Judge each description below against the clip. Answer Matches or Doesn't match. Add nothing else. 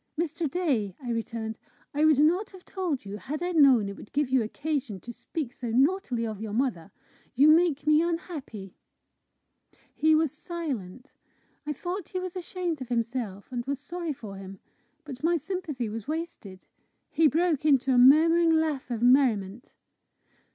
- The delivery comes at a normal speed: Matches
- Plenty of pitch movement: Matches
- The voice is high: Matches